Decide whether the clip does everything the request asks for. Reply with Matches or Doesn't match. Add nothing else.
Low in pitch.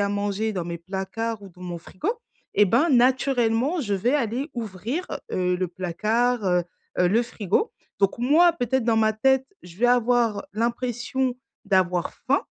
Doesn't match